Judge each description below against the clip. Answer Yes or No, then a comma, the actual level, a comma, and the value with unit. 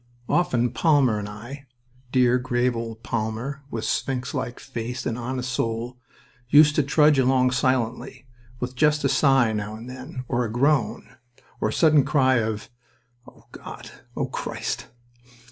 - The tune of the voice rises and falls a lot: No, average, 2.7 semitones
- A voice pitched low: Yes, low, 125 Hz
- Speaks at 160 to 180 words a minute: No, average, 150 wpm